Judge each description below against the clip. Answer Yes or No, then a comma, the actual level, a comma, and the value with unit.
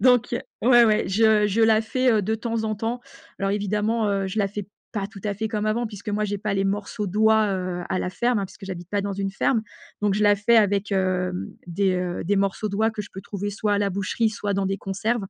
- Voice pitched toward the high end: Yes, high, 205 Hz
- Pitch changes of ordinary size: No, narrow, 2.0 semitones